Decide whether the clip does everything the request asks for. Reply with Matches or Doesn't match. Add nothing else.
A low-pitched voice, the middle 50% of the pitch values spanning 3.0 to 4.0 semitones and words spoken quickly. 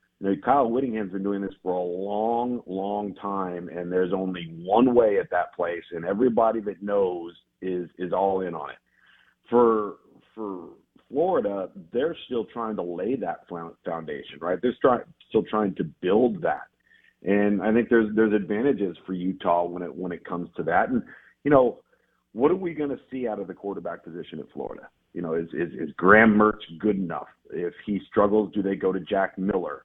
Doesn't match